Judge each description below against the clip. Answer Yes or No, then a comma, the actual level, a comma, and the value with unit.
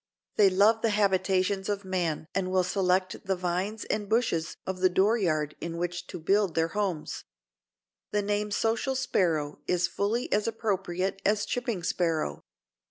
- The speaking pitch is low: No, high, 190 Hz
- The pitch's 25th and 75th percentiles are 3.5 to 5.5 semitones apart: No, average, 2.8 semitones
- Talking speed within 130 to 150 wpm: No, average, 160 wpm